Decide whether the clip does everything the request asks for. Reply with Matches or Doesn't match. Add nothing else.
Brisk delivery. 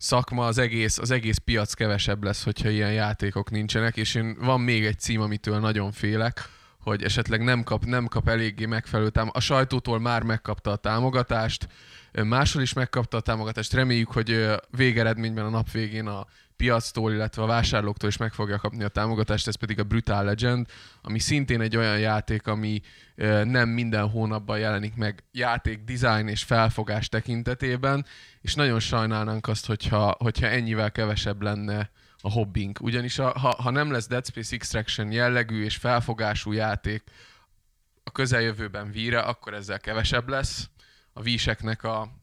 Matches